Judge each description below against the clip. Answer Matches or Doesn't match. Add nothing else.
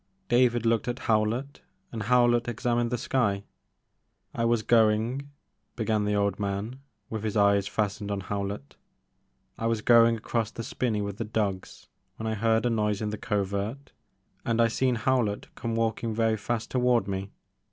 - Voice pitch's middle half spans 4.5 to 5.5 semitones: Doesn't match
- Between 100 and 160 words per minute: Doesn't match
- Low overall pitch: Matches